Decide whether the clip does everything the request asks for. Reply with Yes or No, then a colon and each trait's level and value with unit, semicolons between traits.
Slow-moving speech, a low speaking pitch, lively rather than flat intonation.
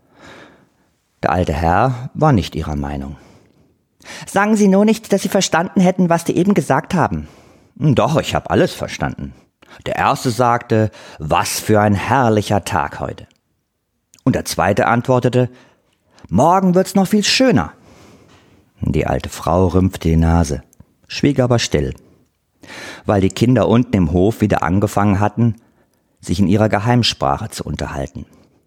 No: average, 140 wpm; low, 110 Hz; wide, 8.6 semitones